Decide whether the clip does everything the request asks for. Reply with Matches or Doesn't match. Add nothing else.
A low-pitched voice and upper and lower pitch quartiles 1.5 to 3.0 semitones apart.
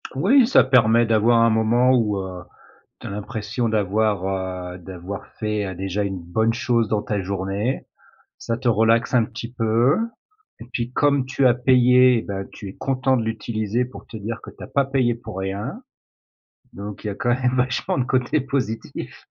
Doesn't match